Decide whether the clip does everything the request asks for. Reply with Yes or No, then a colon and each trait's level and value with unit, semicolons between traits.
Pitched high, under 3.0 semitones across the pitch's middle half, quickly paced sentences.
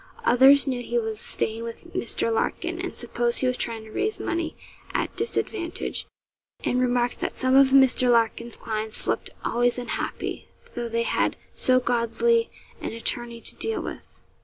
No: high, 245 Hz; narrow, 2.6 semitones; average, 160 wpm